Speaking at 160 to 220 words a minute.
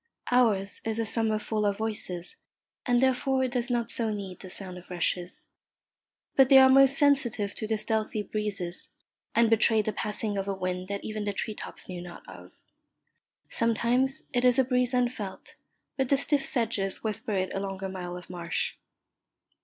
Yes: average, 180 wpm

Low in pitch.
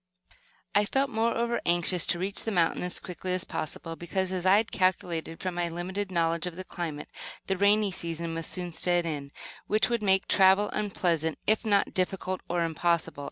No: medium, 180 Hz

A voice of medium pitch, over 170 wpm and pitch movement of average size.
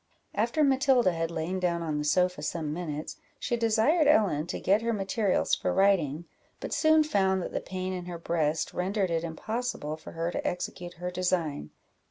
Yes: medium, 180 Hz; average, 185 wpm; average, 4.6 semitones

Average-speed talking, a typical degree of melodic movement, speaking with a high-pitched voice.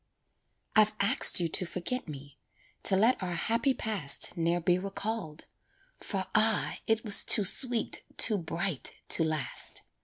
Yes: average, 145 wpm; average, 4.7 semitones; high, 195 Hz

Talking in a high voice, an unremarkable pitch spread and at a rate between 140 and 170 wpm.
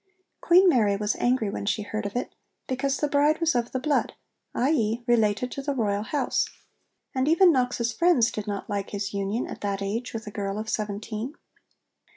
No: high, 230 Hz; average, 4.8 semitones; average, 190 wpm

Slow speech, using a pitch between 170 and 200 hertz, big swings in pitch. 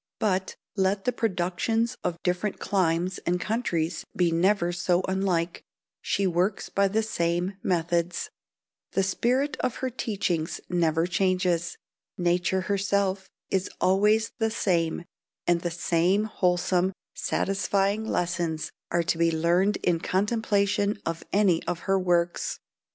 No: slow, 130 wpm; medium, 185 Hz; narrow, 2.6 semitones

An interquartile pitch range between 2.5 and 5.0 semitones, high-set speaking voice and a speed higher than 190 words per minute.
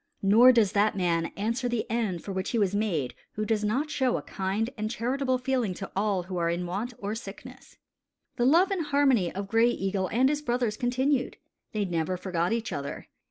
Yes: average, 4.7 semitones; high, 215 Hz; fast, 205 wpm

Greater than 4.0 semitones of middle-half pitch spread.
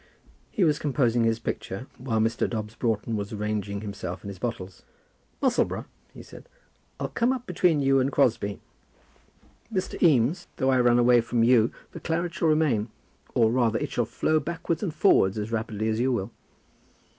Yes: wide, 5.4 semitones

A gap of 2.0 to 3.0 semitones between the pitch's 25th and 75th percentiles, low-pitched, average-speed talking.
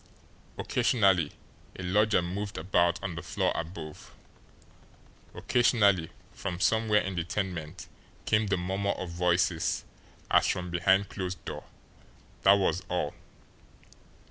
No: narrow, 2.4 semitones; very low, 90 Hz; slow, 115 wpm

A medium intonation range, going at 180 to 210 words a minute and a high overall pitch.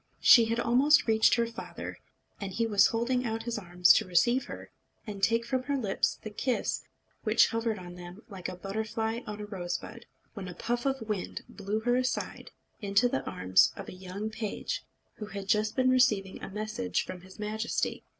Yes: average, 3.2 semitones; average, 190 wpm; high, 215 Hz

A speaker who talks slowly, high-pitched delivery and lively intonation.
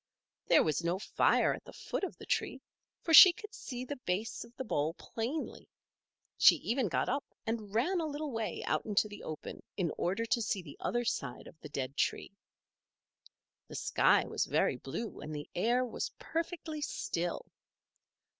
No: average, 180 wpm; high, 225 Hz; wide, 8.2 semitones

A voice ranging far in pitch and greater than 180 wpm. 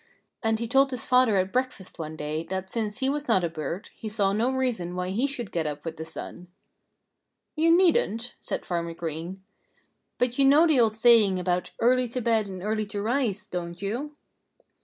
Yes: wide, 5.7 semitones; average, 200 wpm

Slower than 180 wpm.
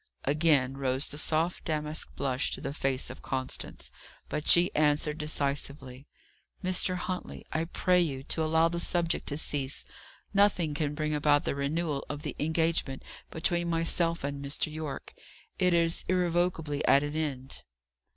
Yes: average, 150 wpm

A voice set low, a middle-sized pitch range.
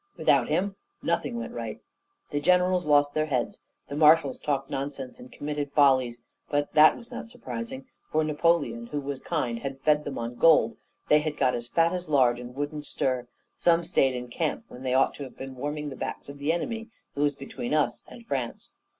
No: medium, 145 Hz; average, 3.2 semitones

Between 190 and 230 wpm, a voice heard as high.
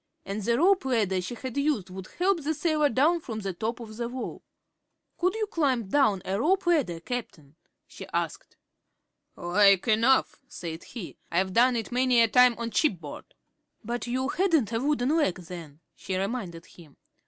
No: average, 175 wpm; high, 235 Hz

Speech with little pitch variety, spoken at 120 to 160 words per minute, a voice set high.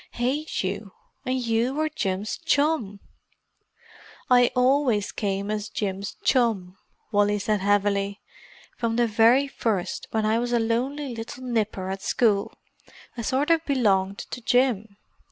No: average, 3.8 semitones; slow, 135 wpm; high, 225 Hz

